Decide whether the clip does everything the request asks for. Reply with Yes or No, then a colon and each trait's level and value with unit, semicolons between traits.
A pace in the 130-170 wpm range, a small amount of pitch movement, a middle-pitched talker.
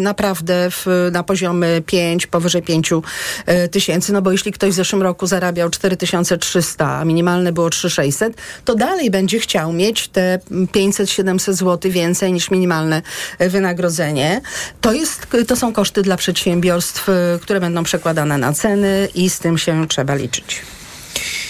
Yes: average, 140 wpm; narrow, 2.3 semitones; medium, 180 Hz